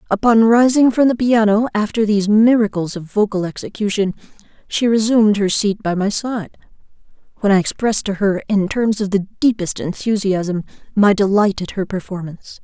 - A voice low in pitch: No, high, 205 Hz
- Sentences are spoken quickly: No, average, 160 wpm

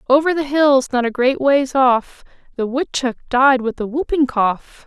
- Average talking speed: Yes, average, 185 wpm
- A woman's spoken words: Yes, female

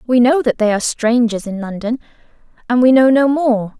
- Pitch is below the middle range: No, high, 240 Hz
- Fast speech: No, average, 190 wpm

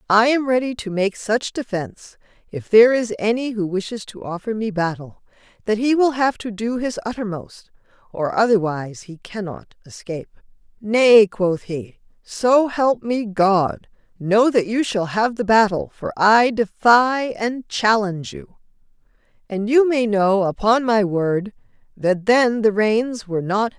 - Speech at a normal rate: Yes, average, 165 wpm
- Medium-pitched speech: No, high, 215 Hz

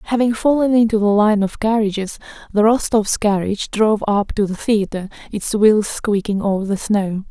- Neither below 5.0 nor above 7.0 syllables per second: Yes, 5.1 syllables/s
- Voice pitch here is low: No, high, 210 Hz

